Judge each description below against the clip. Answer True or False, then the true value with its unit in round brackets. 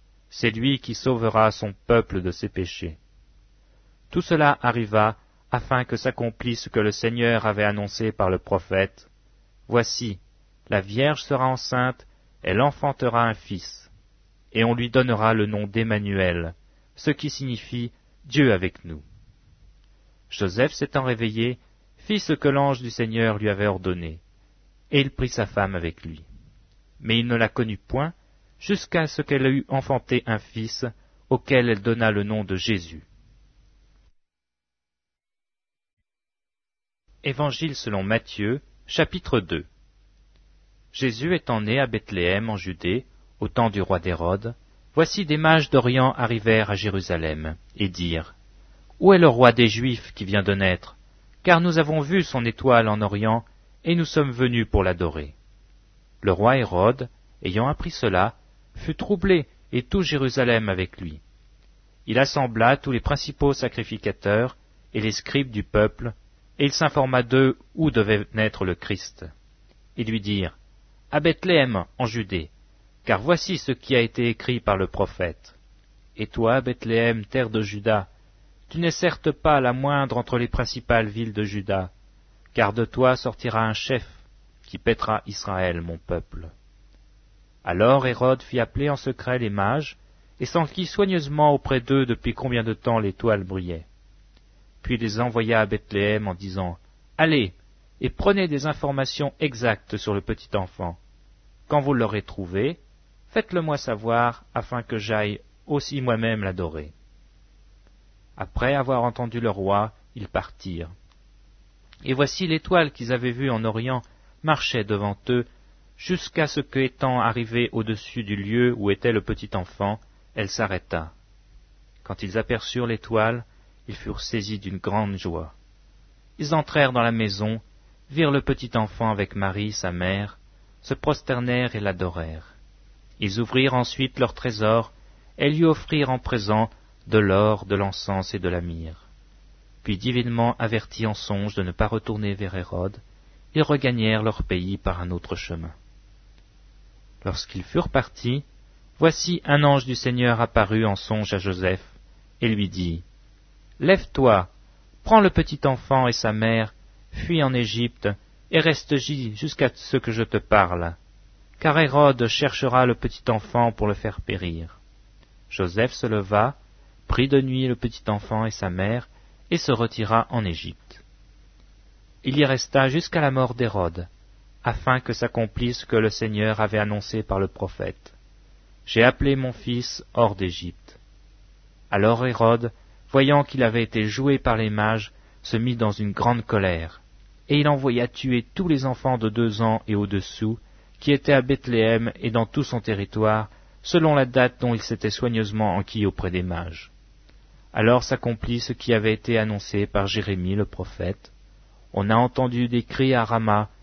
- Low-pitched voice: True (110 Hz)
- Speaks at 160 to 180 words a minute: False (150 wpm)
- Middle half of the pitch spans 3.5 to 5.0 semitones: True (4.4 semitones)